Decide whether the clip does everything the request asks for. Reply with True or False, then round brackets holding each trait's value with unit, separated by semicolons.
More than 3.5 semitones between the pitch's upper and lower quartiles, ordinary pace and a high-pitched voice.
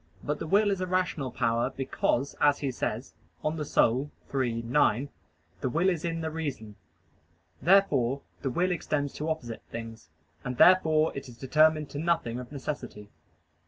False (4.6 semitones; 160 wpm; 145 Hz)